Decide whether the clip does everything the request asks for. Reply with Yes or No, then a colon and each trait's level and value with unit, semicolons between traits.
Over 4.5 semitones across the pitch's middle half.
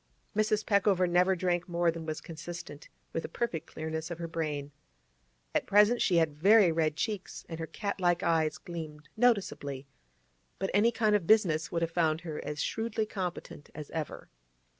No: average, 4.0 semitones